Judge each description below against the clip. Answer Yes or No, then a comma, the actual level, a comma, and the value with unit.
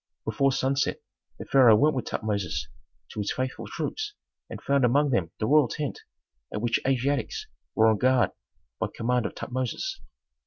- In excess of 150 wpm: Yes, average, 160 wpm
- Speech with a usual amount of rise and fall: Yes, average, 3.5 semitones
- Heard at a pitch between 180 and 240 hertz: No, low, 130 Hz